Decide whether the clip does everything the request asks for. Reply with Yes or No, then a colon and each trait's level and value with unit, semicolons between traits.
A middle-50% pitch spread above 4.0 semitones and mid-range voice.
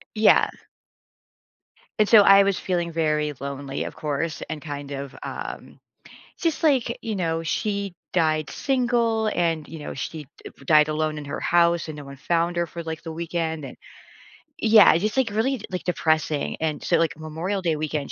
Yes: average, 4.5 semitones; medium, 165 Hz